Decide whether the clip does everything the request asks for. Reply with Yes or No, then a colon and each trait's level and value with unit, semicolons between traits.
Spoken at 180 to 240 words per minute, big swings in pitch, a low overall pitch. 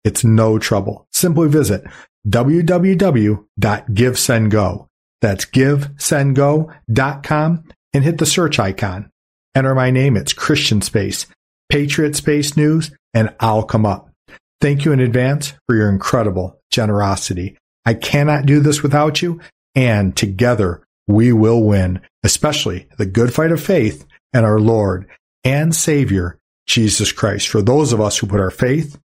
No: average, 140 wpm; wide, 6.0 semitones; low, 120 Hz